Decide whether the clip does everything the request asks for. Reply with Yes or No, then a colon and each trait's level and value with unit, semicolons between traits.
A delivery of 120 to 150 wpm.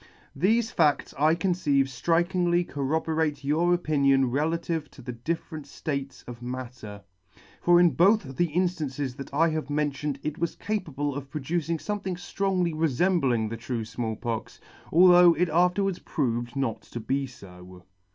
Yes: average, 145 wpm